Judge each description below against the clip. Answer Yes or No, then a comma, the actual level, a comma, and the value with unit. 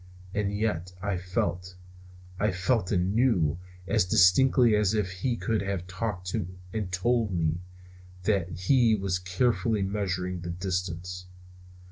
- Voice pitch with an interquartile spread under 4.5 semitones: Yes, average, 2.9 semitones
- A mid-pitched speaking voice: No, very low, 95 Hz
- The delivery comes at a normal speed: No, slow, 130 wpm